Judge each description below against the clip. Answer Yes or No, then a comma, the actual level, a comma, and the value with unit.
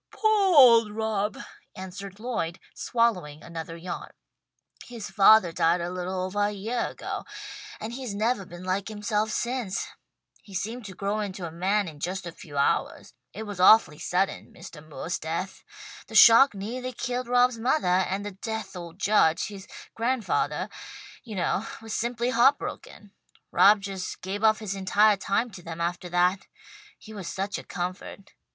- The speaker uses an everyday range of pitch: Yes, average, 3.7 semitones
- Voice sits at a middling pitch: No, high, 200 Hz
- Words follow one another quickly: No, average, 160 wpm